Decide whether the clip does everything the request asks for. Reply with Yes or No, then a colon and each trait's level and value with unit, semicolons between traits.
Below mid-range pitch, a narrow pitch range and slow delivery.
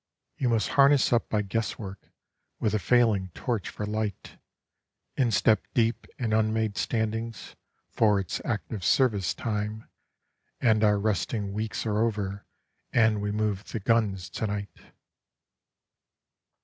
Yes: low, 110 Hz; narrow, 1.8 semitones; slow, 125 wpm